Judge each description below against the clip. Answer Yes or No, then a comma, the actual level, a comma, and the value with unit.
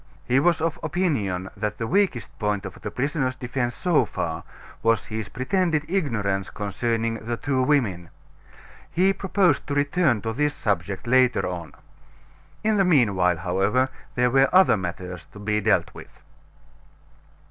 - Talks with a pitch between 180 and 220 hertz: No, low, 120 Hz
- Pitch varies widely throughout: Yes, wide, 6.6 semitones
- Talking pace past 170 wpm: No, average, 150 wpm